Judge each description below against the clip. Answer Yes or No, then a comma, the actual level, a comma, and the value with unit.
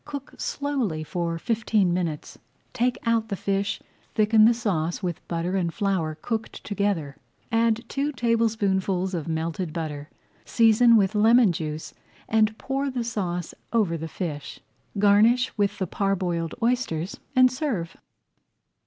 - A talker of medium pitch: No, high, 200 Hz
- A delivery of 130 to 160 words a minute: Yes, slow, 135 wpm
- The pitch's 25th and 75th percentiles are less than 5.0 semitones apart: No, average, 5.3 semitones